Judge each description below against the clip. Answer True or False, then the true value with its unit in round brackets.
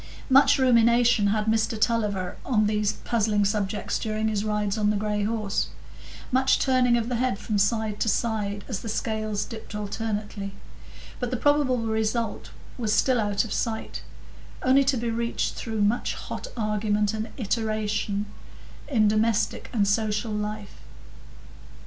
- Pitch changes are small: True (2.0 semitones)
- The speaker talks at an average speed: True (150 wpm)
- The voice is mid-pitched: False (215 Hz)